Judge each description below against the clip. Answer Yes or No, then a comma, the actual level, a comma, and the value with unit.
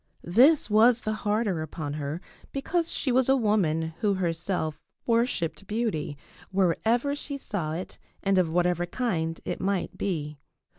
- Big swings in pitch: Yes, wide, 6.1 semitones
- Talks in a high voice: Yes, high, 195 Hz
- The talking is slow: No, average, 145 wpm